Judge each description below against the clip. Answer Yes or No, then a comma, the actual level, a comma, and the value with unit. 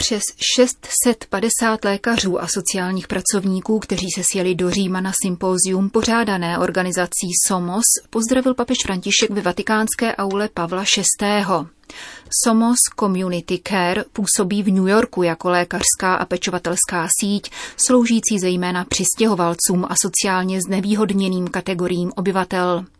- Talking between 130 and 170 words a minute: No, slow, 115 wpm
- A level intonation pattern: No, average, 3.0 semitones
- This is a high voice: Yes, high, 195 Hz